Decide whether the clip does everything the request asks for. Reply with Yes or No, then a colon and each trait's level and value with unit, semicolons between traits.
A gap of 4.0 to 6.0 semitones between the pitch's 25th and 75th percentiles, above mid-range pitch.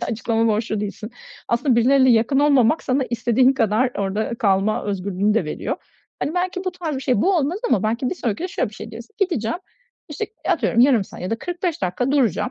Yes: average, 4.9 semitones; high, 235 Hz